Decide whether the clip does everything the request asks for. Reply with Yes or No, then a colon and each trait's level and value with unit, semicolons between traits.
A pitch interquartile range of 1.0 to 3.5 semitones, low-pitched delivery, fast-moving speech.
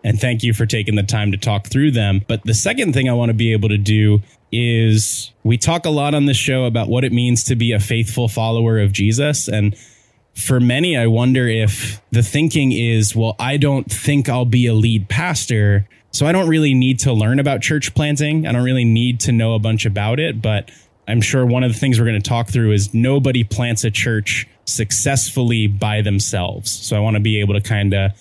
Yes: average, 2.9 semitones; low, 115 Hz; fast, 230 wpm